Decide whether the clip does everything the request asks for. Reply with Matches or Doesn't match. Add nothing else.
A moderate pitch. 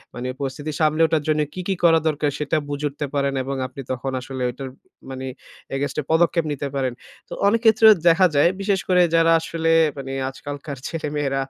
Matches